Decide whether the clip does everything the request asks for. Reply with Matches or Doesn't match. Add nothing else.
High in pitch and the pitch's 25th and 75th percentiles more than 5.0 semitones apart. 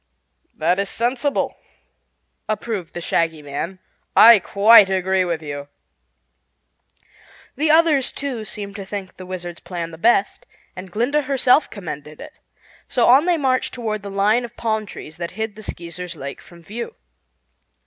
Matches